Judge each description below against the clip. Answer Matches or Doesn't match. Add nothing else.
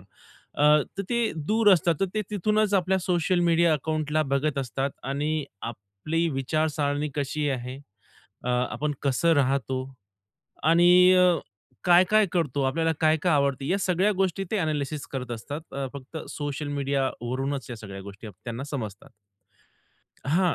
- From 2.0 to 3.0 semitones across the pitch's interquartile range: Doesn't match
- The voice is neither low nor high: Matches